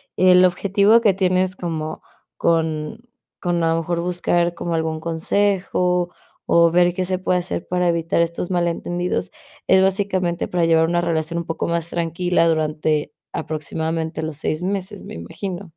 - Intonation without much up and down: Yes, narrow, 1.9 semitones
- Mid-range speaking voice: Yes, medium, 170 Hz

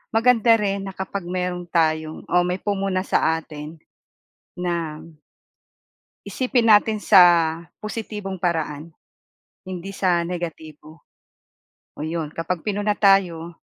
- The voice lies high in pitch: No, medium, 180 Hz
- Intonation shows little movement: No, average, 3.5 semitones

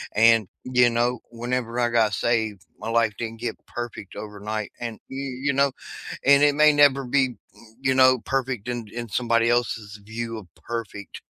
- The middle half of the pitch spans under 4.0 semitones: Yes, narrow, 2.4 semitones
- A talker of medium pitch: No, low, 120 Hz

